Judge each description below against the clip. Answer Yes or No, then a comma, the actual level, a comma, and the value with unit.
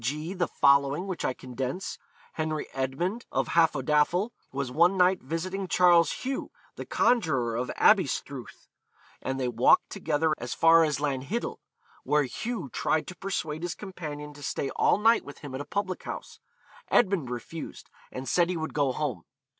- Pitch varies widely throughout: No, average, 5.0 semitones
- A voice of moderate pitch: Yes, medium, 155 Hz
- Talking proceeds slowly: No, average, 160 wpm